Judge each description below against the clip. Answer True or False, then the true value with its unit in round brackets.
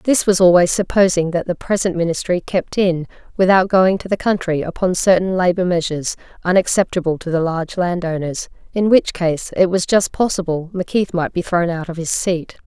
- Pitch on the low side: False (180 Hz)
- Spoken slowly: False (190 wpm)